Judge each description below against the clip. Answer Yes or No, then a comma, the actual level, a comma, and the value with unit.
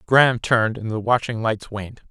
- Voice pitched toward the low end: Yes, low, 115 Hz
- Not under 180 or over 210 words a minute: Yes, average, 200 wpm